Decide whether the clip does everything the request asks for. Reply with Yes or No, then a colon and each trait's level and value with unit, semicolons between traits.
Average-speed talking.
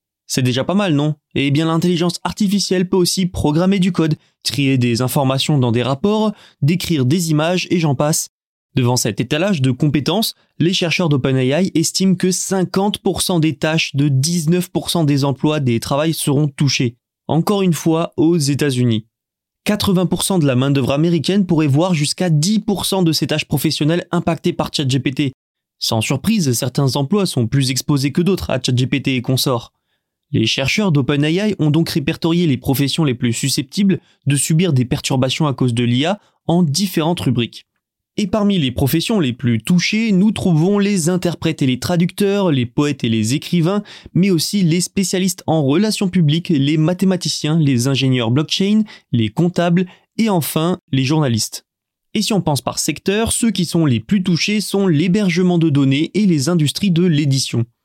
Yes: average, 170 wpm